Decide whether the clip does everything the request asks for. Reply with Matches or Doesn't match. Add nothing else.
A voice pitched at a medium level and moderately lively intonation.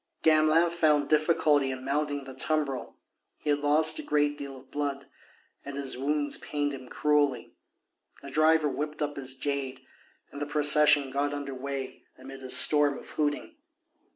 Doesn't match